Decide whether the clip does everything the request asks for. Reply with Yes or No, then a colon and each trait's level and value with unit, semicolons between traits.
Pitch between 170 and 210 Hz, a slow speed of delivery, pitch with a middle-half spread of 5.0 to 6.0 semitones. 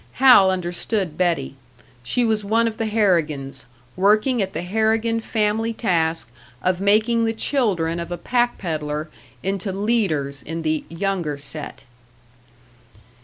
Yes: high, 190 Hz; slow, 130 wpm; wide, 5.4 semitones